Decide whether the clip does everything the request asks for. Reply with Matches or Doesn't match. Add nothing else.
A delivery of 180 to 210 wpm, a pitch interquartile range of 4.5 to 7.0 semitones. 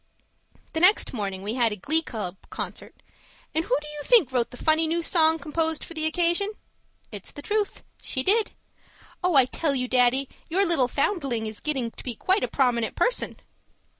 Matches